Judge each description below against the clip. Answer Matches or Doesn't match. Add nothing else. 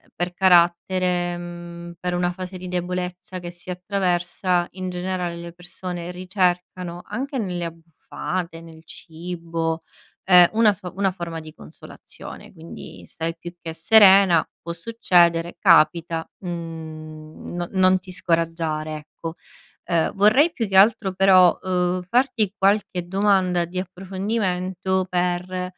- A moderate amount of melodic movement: Doesn't match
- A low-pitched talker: Doesn't match